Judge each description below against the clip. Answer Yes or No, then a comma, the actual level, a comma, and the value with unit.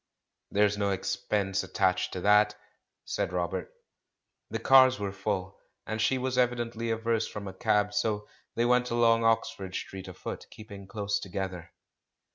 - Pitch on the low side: Yes, low, 105 Hz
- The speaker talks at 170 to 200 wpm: No, average, 145 wpm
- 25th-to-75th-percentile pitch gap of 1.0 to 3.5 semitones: Yes, average, 2.9 semitones